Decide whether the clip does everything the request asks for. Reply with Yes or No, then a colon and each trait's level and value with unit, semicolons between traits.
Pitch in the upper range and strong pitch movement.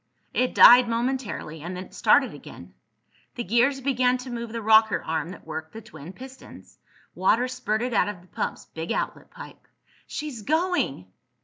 Yes: high, 230 Hz; wide, 5.7 semitones